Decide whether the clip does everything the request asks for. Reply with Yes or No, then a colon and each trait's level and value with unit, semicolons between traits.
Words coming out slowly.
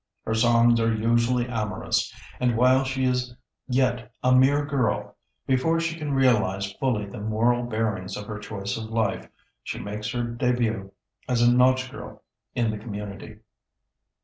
No: average, 155 wpm